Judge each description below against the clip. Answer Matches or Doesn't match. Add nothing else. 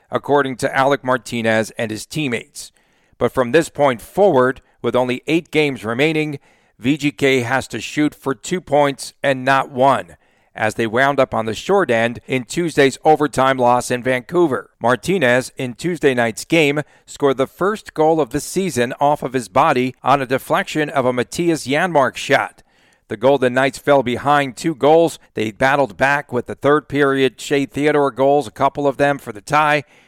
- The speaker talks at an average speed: Matches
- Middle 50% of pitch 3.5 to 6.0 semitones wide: Doesn't match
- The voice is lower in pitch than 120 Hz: Doesn't match